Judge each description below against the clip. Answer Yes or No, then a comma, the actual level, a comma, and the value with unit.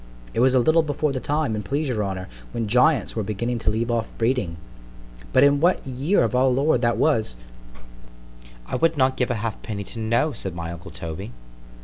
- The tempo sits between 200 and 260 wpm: Yes, fast, 205 wpm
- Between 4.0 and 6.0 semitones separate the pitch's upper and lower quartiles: Yes, average, 5.2 semitones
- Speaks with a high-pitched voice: No, low, 120 Hz